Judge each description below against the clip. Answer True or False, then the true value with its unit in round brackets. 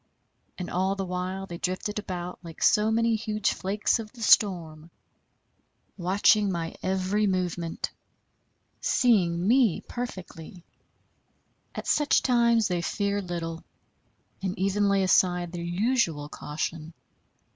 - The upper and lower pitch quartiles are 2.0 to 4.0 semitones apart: True (3.4 semitones)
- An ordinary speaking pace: False (120 wpm)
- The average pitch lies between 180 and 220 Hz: True (190 Hz)